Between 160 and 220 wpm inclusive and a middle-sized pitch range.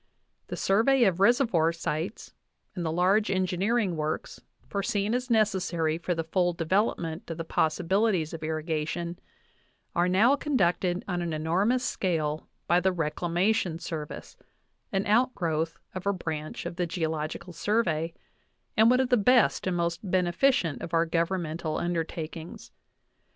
No: average, 145 wpm; average, 3.6 semitones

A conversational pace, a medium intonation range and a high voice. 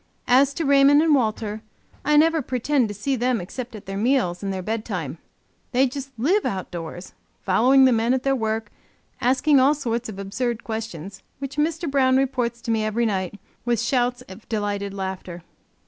Yes: average, 180 wpm; average, 4.7 semitones; high, 235 Hz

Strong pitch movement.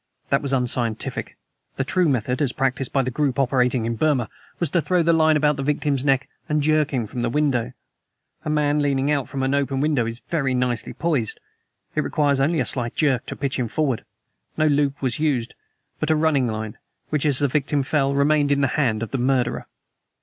No: average, 3.0 semitones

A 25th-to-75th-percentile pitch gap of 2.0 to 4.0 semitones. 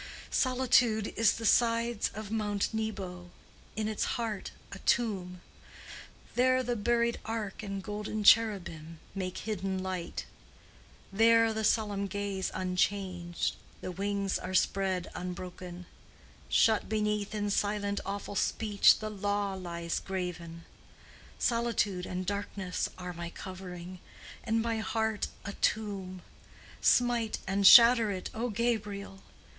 Yes: average, 2.9 semitones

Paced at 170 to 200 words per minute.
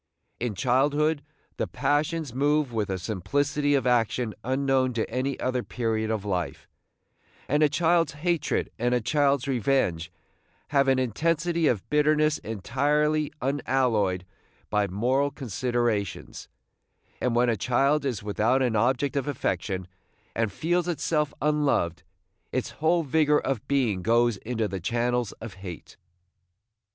No: slow, 135 wpm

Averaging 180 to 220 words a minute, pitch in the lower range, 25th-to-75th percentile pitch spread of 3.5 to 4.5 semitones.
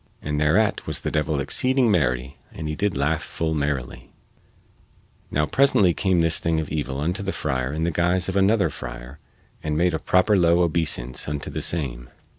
Yes: average, 185 wpm; very low, 80 Hz; average, 3.9 semitones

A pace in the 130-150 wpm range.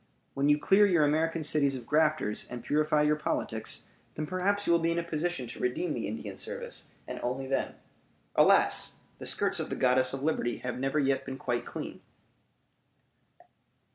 No: average, 180 wpm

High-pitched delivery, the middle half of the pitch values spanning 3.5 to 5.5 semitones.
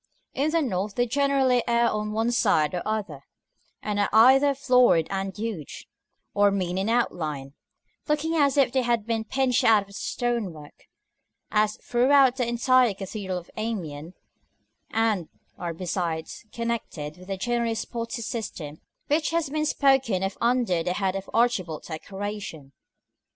Yes: high, 220 Hz; average, 4.9 semitones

